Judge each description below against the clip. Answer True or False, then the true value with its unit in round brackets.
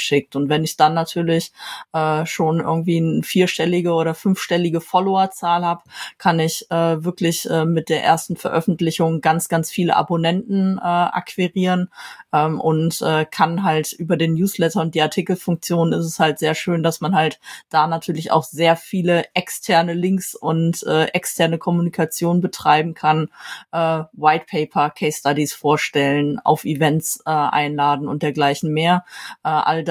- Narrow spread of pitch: True (1.9 semitones)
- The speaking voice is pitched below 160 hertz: False (165 Hz)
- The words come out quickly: False (155 wpm)